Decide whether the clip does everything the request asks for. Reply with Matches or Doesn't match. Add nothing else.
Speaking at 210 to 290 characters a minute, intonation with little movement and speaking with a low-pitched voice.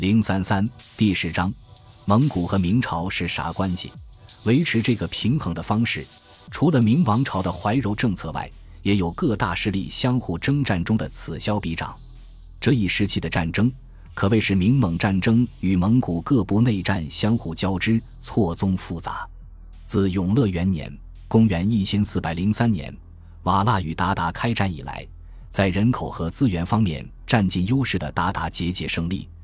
Doesn't match